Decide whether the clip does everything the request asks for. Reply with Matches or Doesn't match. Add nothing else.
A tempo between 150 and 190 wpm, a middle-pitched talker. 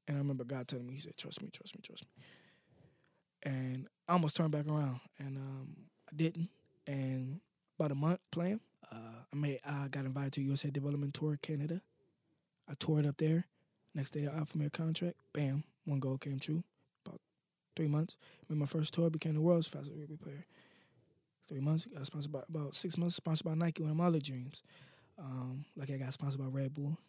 Doesn't match